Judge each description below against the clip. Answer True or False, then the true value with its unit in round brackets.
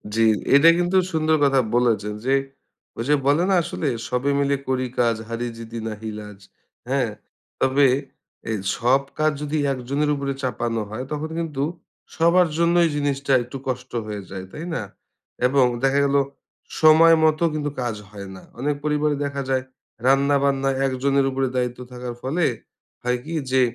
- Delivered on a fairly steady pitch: False (3.3 semitones)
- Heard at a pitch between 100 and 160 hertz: True (135 Hz)